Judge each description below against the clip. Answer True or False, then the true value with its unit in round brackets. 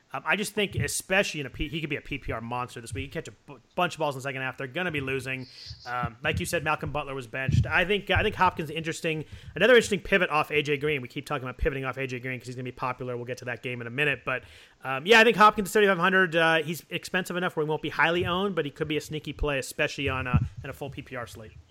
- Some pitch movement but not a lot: True (4.3 semitones)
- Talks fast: True (290 wpm)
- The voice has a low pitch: False (145 Hz)